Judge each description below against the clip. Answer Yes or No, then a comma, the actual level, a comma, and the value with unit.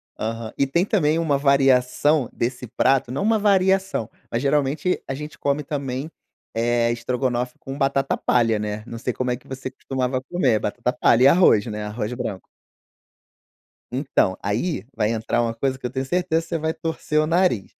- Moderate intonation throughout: Yes, average, 4.1 semitones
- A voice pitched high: No, low, 130 Hz